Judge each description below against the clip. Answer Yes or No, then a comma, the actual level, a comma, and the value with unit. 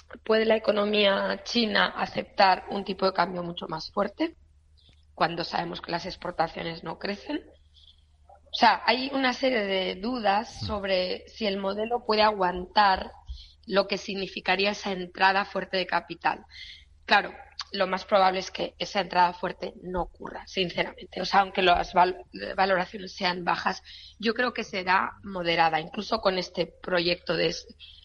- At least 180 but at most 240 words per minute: No, average, 150 wpm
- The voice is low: No, high, 190 Hz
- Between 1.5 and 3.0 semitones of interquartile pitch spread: Yes, narrow, 2.6 semitones